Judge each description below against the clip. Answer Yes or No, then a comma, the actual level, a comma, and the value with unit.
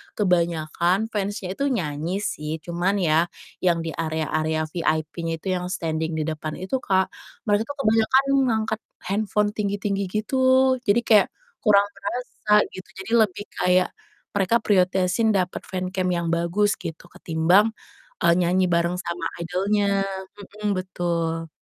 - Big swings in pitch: No, average, 3.5 semitones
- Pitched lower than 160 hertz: No, medium, 185 Hz